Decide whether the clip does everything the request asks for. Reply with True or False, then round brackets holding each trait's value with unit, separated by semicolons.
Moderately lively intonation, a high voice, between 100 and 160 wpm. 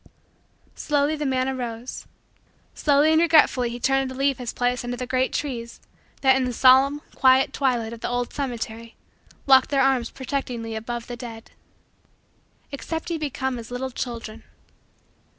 False (2.2 semitones; 255 Hz; 155 wpm)